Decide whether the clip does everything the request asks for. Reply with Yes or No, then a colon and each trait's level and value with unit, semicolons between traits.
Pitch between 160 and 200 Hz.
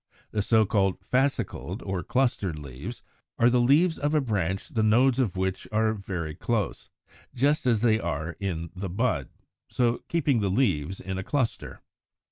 No: low, 110 Hz